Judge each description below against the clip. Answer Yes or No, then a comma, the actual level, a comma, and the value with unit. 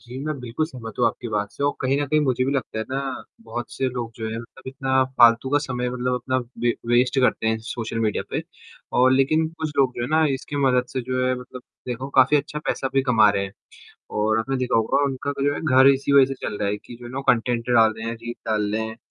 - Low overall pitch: Yes, low, 125 Hz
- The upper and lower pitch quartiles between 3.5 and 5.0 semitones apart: No, average, 2.7 semitones